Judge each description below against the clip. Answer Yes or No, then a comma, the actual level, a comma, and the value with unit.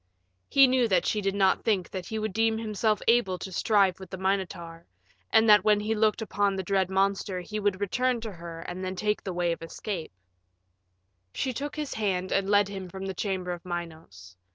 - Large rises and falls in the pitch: No, average, 2.9 semitones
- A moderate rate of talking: No, fast, 215 wpm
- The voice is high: Yes, high, 195 Hz